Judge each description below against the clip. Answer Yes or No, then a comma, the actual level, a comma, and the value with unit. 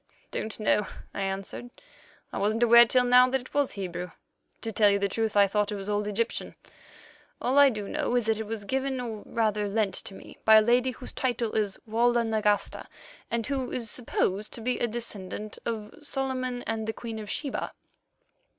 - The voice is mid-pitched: No, high, 225 Hz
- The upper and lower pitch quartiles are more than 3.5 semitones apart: No, average, 2.8 semitones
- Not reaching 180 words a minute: No, average, 195 wpm